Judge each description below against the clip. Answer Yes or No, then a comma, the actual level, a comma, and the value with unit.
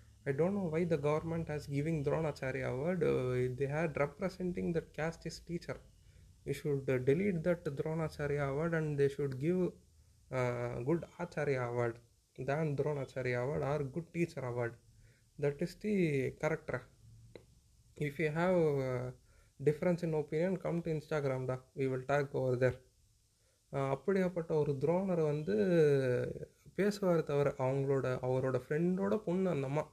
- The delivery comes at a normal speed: No, fast, 135 wpm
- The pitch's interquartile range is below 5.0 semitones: Yes, average, 4.4 semitones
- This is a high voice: No, medium, 145 Hz